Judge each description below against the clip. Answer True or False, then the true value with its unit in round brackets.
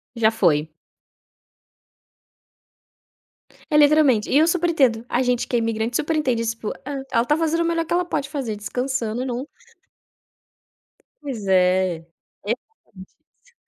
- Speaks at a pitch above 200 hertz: True (250 Hz)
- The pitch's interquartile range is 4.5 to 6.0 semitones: True (5.4 semitones)